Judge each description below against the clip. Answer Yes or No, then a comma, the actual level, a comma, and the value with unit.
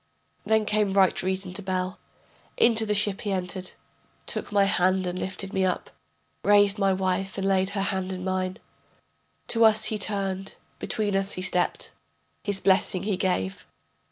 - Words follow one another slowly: No, average, 165 wpm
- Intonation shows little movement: Yes, narrow, 1.6 semitones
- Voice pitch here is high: Yes, high, 195 Hz